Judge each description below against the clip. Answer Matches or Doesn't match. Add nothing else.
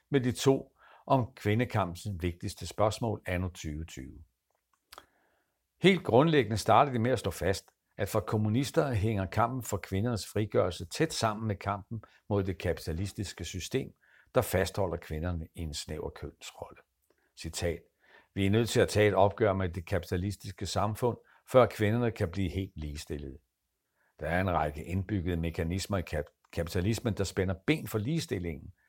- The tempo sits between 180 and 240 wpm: Doesn't match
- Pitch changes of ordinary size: Matches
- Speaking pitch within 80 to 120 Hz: Matches